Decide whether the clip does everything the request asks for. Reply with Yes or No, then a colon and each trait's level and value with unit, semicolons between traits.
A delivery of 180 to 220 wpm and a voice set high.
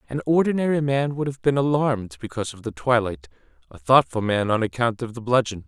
No: average, 200 wpm; low, 125 Hz